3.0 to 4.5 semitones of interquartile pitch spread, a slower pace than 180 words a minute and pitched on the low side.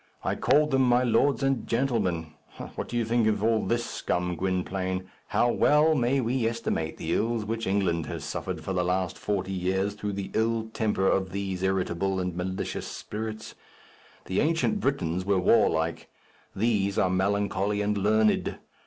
Yes: average, 3.8 semitones; average, 165 wpm; low, 100 Hz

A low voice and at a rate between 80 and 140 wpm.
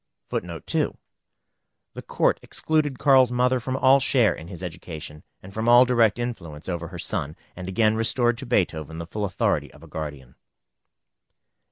No: low, 105 Hz; average, 170 wpm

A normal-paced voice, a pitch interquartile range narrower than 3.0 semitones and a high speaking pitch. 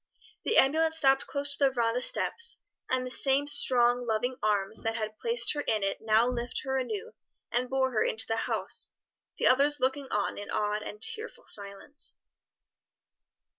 No: average, 170 wpm; average, 4.2 semitones; very high, 250 Hz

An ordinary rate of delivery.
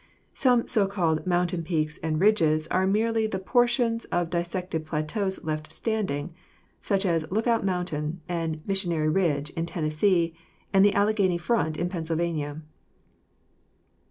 No: slow, 130 wpm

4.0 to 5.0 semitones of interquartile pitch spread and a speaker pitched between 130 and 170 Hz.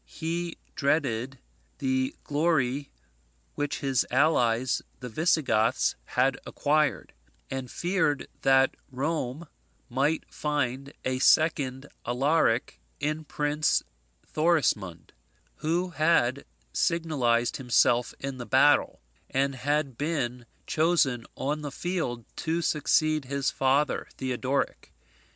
No: average, 3.4 semitones; medium, 140 Hz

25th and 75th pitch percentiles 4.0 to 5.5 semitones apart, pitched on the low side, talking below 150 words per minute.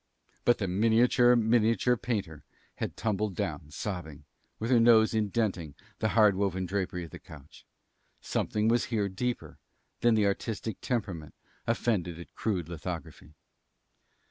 Yes: average, 4.5 semitones; low, 105 Hz; slow, 135 wpm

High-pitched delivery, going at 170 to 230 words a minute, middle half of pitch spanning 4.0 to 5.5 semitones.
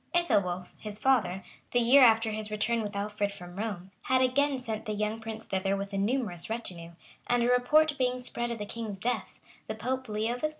No: high, 220 Hz; fast, 205 wpm; average, 3.6 semitones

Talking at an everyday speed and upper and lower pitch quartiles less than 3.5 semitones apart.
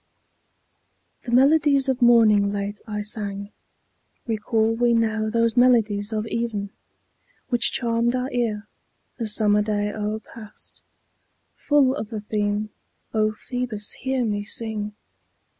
No: slow, 120 wpm; narrow, 2.4 semitones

